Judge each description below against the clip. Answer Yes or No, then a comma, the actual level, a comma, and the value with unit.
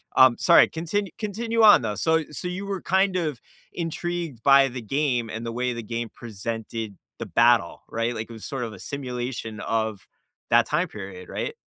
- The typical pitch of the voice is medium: No, low, 125 Hz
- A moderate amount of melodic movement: No, wide, 7.1 semitones